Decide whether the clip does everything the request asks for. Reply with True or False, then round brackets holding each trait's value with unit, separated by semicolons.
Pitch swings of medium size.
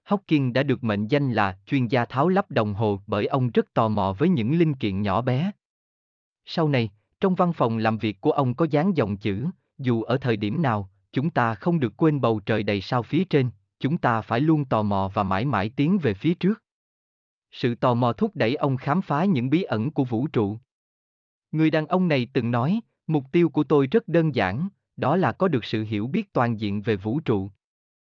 False (6.9 semitones)